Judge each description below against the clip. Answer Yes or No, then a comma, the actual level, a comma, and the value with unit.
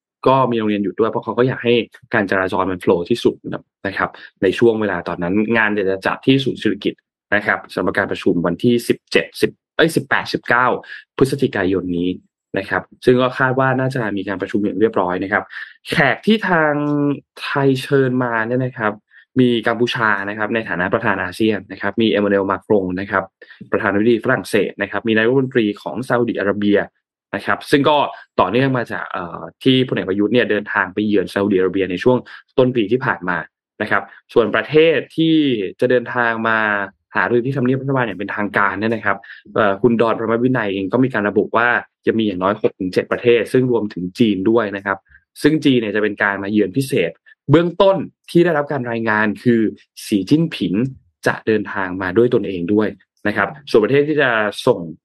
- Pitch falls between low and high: No, low, 110 Hz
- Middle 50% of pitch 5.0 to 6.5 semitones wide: No, average, 4.3 semitones